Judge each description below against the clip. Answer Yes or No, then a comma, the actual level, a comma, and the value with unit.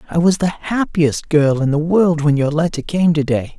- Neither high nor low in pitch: Yes, medium, 160 Hz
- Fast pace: Yes, fast, 220 wpm